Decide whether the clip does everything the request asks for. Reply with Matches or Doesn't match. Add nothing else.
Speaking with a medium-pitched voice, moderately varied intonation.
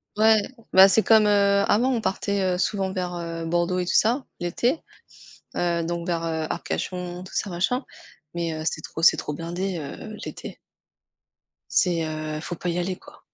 Matches